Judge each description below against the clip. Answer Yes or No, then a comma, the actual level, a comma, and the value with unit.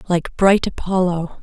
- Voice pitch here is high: No, medium, 180 Hz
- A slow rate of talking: Yes, slow, 125 wpm